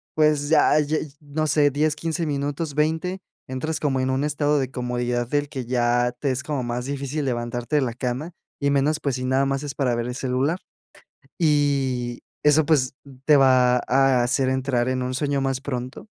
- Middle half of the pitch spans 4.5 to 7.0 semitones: No, average, 2.8 semitones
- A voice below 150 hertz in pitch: Yes, low, 135 Hz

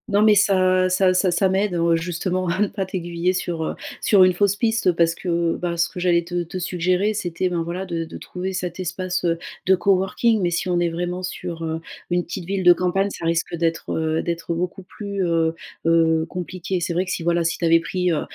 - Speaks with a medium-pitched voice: Yes, medium, 180 Hz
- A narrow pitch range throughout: Yes, narrow, 1.7 semitones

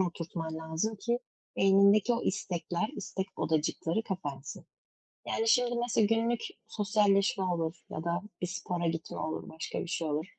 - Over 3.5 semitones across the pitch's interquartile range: Yes, average, 4.6 semitones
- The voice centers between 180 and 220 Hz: Yes, medium, 185 Hz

